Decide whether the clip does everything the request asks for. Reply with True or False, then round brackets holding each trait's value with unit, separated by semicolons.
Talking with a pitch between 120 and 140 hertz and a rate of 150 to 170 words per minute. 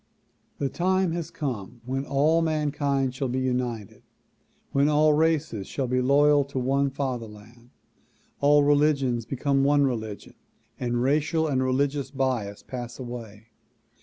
False (135 Hz; 135 wpm)